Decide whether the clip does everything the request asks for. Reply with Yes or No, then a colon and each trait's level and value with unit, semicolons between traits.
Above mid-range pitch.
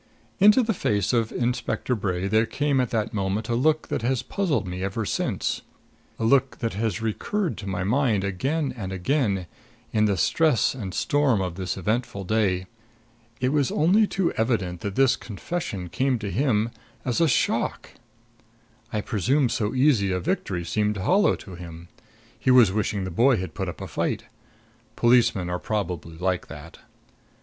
No: low, 110 Hz